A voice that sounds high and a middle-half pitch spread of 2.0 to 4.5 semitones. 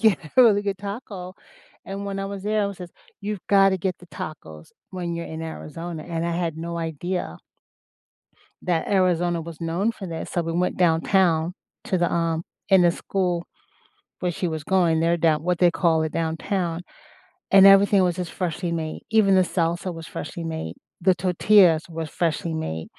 No: medium, 175 Hz; narrow, 2.6 semitones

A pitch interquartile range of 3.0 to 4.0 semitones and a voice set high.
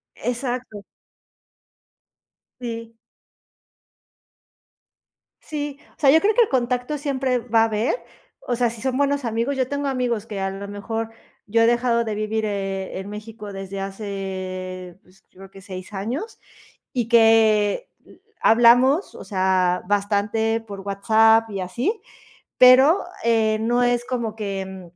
Yes: average, 3.7 semitones; high, 225 Hz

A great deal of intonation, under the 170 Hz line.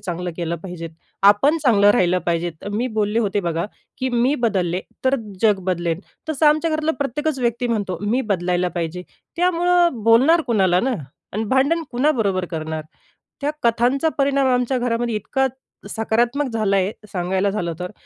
No: wide, 6.5 semitones; high, 225 Hz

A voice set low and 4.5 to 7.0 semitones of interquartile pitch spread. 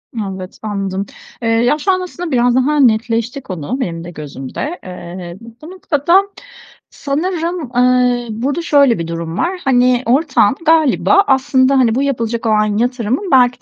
No: high, 245 Hz; average, 5.1 semitones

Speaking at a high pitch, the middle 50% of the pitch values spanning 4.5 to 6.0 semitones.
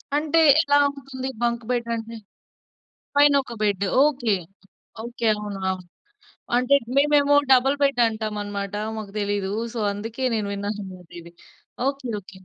Yes: high, 230 Hz; average, 5.1 semitones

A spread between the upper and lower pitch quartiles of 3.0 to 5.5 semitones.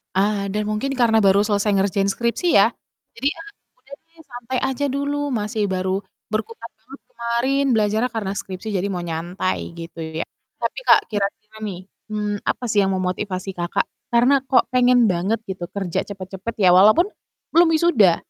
Yes: average, 4.2 semitones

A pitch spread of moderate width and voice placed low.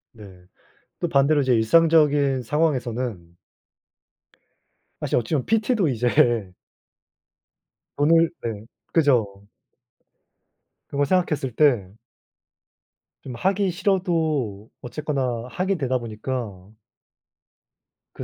No: wide, 6.1 semitones; low, 130 Hz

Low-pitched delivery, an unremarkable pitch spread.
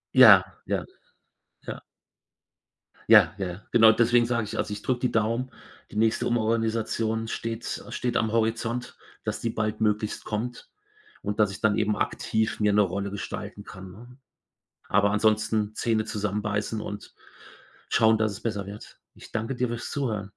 No: low, 110 Hz; narrow, 1.7 semitones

